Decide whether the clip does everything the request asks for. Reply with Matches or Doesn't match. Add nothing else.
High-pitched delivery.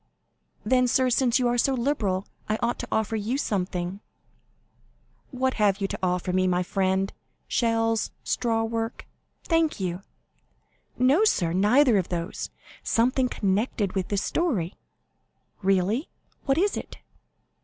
Matches